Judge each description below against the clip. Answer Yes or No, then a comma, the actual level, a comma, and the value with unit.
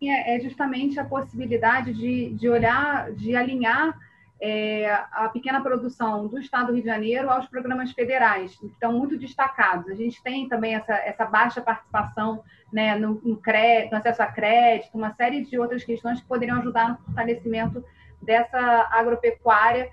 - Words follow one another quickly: No, average, 165 wpm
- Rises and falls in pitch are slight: Yes, narrow, 2.3 semitones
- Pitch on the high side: Yes, high, 235 Hz